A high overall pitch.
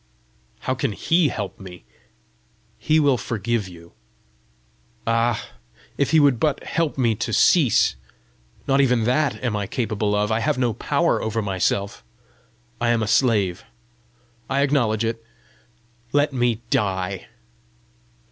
No: low, 115 Hz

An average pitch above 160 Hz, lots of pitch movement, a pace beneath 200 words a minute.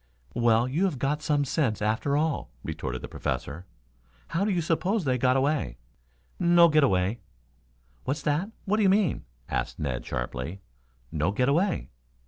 No: medium, 140 Hz; wide, 7.5 semitones; average, 160 wpm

